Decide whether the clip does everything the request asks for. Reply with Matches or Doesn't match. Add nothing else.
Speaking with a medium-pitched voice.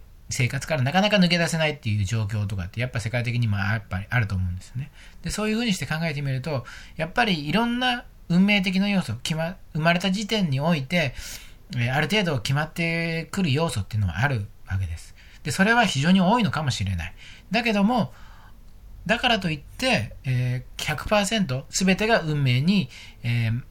Matches